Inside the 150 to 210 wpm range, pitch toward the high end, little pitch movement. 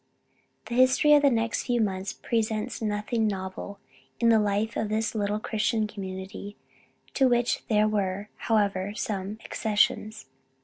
No: average, 140 wpm; high, 215 Hz; narrow, 2.1 semitones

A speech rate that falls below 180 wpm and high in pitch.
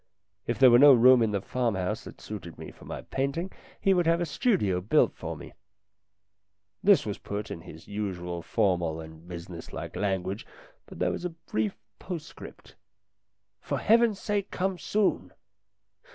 No: average, 165 wpm; low, 110 Hz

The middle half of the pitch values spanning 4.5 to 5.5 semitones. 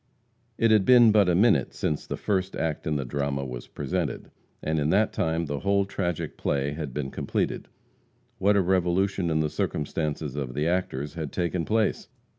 Yes: average, 4.9 semitones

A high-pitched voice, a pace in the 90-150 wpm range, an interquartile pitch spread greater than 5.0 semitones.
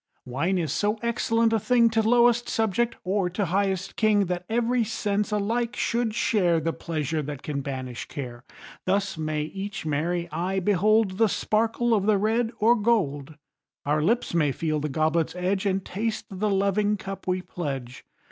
No: high, 195 Hz; average, 170 wpm; wide, 5.5 semitones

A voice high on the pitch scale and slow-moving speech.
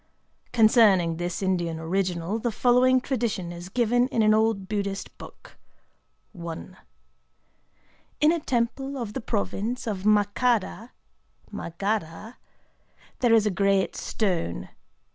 Yes: high, 210 Hz; slow, 105 wpm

